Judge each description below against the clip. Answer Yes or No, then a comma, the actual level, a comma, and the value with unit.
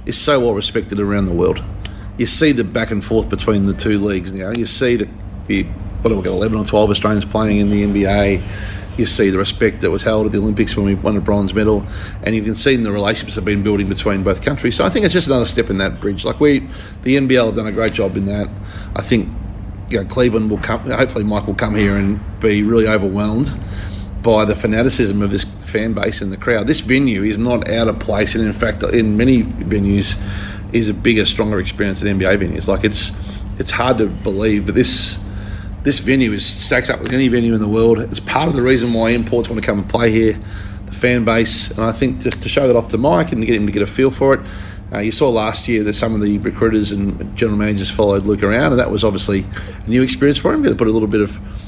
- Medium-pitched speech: No, low, 105 Hz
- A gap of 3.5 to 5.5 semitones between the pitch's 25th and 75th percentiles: No, narrow, 2.5 semitones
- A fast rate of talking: Yes, fast, 250 wpm